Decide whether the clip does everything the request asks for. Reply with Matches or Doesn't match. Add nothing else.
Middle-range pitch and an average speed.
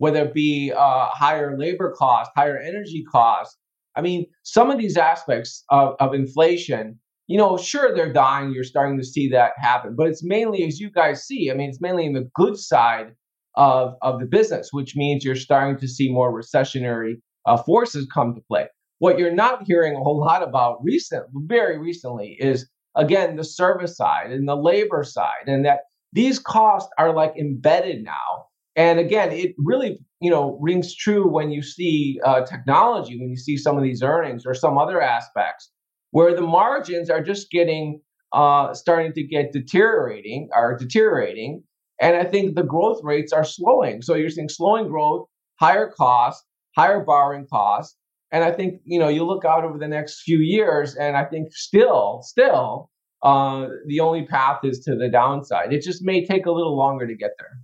Matches